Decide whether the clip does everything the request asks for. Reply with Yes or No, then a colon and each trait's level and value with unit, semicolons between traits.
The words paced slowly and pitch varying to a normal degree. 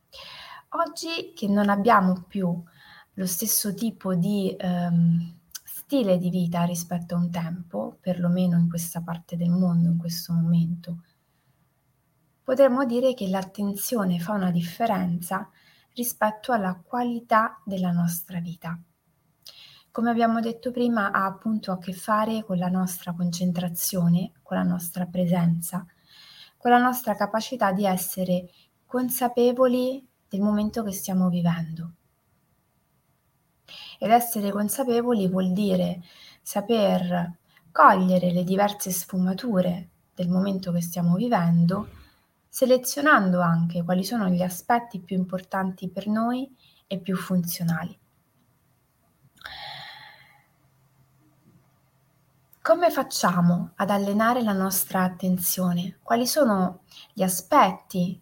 Yes: slow, 110 wpm; average, 3.8 semitones